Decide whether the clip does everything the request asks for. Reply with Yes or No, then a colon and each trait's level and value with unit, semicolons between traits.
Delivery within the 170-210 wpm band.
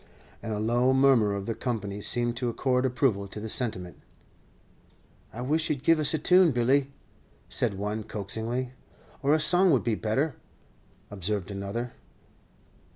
No: average, 155 wpm